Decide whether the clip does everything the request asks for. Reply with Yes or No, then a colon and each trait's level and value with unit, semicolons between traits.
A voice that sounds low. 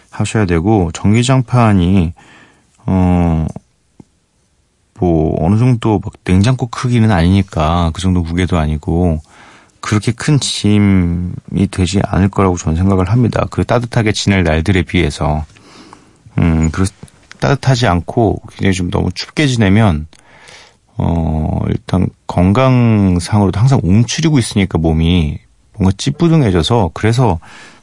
Yes: very low, 95 Hz